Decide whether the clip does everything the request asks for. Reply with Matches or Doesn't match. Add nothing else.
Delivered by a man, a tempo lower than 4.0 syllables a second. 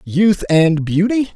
Matches